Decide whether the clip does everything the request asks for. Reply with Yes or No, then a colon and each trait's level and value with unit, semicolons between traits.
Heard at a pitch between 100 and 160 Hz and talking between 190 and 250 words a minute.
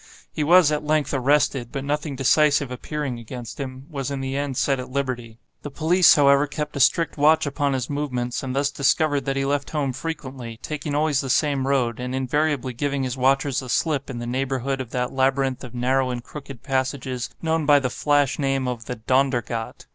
Yes: low, 135 Hz; average, 200 wpm